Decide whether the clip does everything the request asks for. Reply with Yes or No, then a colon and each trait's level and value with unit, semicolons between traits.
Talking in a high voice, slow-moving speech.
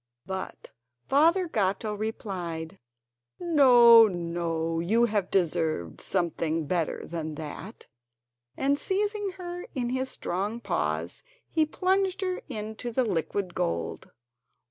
Yes: high, 210 Hz; slow, 110 wpm